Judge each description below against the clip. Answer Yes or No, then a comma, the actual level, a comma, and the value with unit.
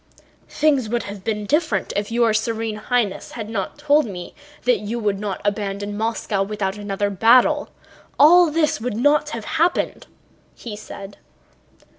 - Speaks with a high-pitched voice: Yes, high, 220 Hz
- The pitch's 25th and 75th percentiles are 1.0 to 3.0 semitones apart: No, average, 3.5 semitones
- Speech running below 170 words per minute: Yes, average, 150 wpm